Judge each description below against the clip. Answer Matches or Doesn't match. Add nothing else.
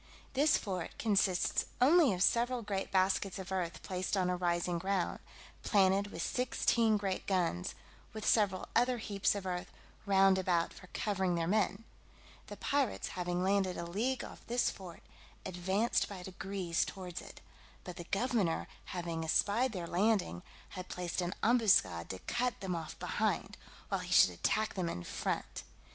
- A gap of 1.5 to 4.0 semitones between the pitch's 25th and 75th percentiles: Matches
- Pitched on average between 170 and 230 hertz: Matches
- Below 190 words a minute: Matches